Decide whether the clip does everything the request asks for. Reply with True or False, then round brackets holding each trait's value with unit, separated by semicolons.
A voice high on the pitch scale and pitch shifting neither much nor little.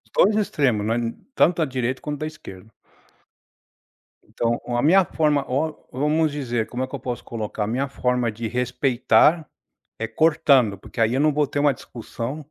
False (130 Hz; 4.2 semitones)